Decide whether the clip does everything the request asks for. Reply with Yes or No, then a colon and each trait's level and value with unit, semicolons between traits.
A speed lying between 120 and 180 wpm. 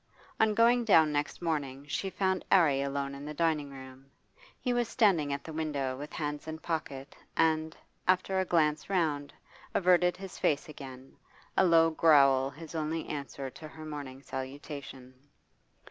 Yes: average, 160 wpm